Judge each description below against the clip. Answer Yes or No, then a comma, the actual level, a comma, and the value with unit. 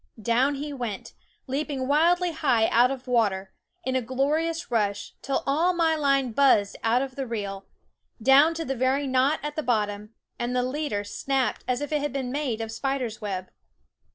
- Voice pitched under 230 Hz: No, very high, 260 Hz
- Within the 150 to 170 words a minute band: No, average, 180 wpm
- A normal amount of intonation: Yes, average, 4.1 semitones